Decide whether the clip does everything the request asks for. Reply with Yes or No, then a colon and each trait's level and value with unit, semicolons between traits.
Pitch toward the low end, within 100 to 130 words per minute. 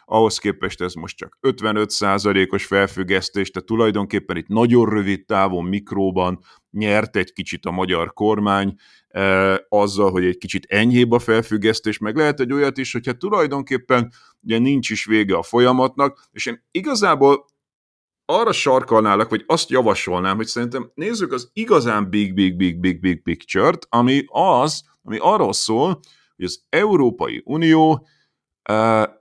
No: low, 110 Hz; average, 150 wpm